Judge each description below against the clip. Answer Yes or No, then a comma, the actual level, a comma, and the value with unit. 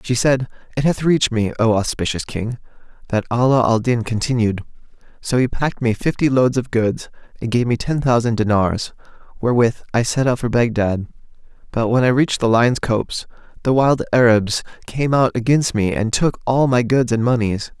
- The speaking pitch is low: Yes, low, 120 Hz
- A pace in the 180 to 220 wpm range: Yes, average, 185 wpm